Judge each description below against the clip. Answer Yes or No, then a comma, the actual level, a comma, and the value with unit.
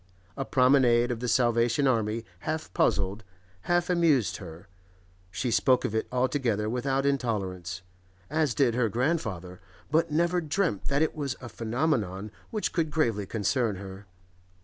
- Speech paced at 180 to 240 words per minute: No, average, 145 wpm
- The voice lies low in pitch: Yes, low, 120 Hz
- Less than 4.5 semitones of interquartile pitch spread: No, average, 5.3 semitones